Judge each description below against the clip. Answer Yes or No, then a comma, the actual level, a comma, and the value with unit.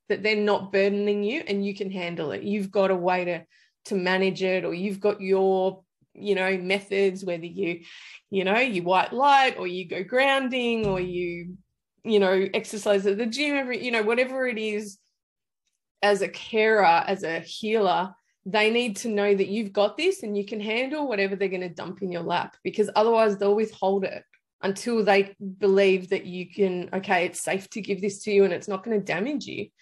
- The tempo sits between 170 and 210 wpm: Yes, fast, 205 wpm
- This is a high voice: Yes, high, 200 Hz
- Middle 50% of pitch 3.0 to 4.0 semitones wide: No, narrow, 2.4 semitones